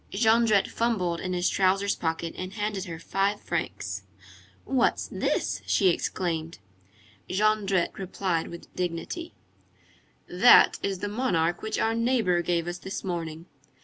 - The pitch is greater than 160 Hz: Yes, medium, 185 Hz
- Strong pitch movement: No, average, 3.6 semitones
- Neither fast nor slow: No, slow, 130 wpm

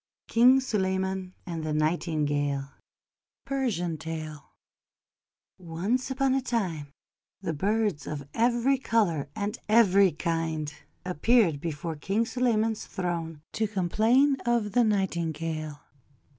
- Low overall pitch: No, medium, 185 Hz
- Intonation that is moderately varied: No, wide, 6.2 semitones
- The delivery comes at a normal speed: No, slow, 105 wpm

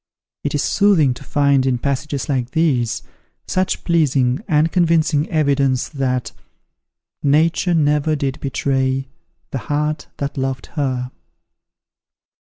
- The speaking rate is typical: No, slow, 115 wpm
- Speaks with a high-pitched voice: No, medium, 140 Hz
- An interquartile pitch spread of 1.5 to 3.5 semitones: Yes, average, 2.7 semitones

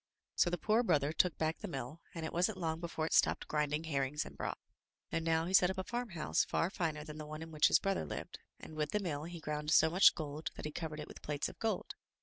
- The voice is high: No, medium, 160 Hz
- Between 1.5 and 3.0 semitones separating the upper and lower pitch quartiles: Yes, average, 2.7 semitones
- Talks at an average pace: No, fast, 260 wpm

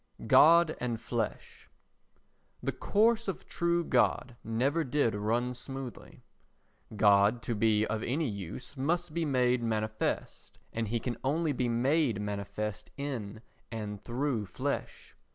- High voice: No, low, 120 Hz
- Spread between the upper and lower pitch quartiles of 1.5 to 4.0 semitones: No, average, 5.0 semitones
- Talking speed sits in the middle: No, slow, 130 wpm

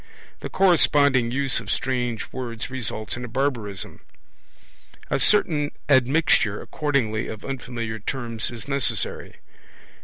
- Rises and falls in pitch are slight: No, average, 3.6 semitones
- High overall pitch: No, low, 125 Hz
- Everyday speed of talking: No, slow, 115 wpm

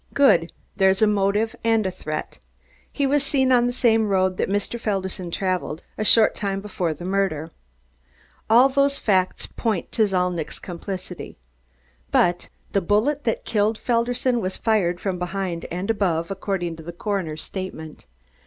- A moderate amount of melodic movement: Yes, average, 3.9 semitones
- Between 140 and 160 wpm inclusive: Yes, average, 155 wpm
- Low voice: No, high, 195 Hz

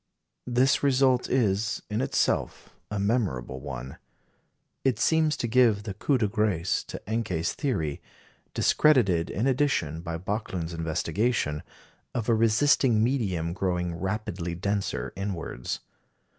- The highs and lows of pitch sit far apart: Yes, wide, 6.2 semitones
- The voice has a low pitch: Yes, low, 105 Hz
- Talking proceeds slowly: Yes, slow, 120 wpm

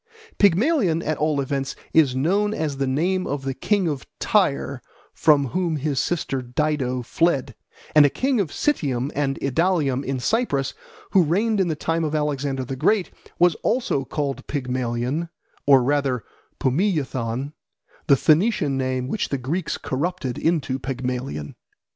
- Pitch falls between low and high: Yes, medium, 145 Hz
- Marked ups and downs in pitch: No, average, 4.6 semitones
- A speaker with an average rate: Yes, average, 150 wpm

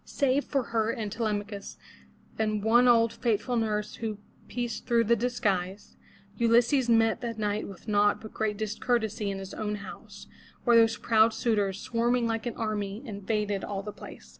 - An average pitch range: No, narrow, 2.2 semitones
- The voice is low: No, high, 220 Hz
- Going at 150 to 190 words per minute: Yes, average, 170 wpm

